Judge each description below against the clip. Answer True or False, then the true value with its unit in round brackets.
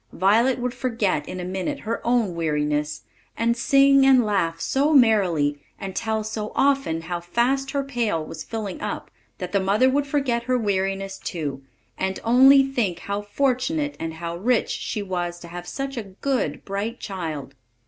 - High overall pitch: True (210 Hz)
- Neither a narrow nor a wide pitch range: False (6.4 semitones)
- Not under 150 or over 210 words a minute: True (170 wpm)